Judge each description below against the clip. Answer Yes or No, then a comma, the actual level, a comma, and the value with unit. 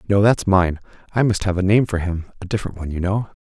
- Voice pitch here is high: No, very low, 95 Hz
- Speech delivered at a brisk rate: Yes, fast, 245 wpm